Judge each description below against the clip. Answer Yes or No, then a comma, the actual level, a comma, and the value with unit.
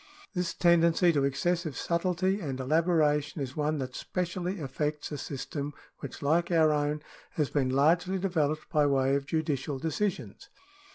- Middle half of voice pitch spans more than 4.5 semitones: No, average, 3.4 semitones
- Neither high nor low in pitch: Yes, medium, 155 Hz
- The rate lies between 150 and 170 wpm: Yes, average, 155 wpm